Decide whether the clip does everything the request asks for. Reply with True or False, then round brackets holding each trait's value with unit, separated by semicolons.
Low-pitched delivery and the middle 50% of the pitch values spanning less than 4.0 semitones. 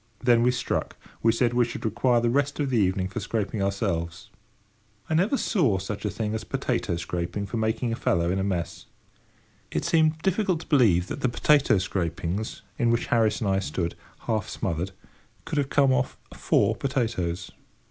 False (110 Hz; 5.1 semitones)